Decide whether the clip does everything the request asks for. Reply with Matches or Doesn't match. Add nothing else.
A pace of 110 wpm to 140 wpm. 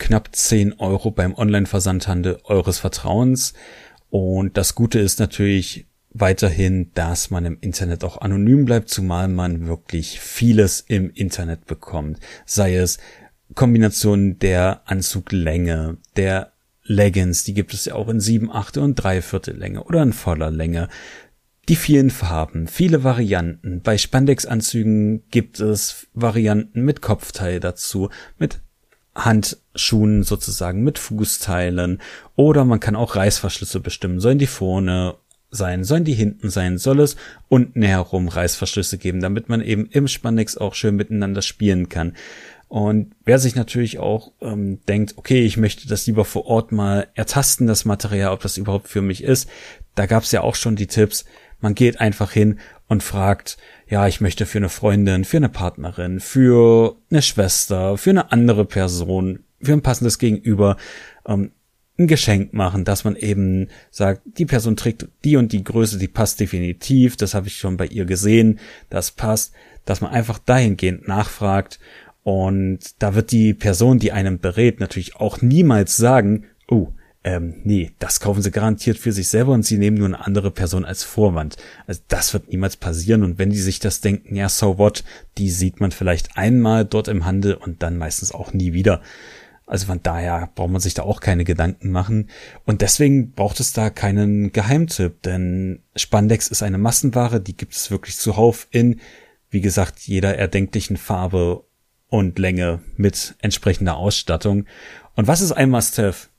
Doesn't match